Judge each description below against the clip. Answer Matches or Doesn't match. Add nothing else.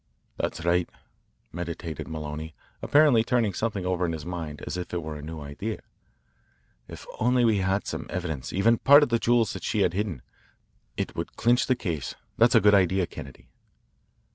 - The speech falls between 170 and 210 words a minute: Matches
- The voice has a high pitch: Doesn't match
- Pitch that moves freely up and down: Matches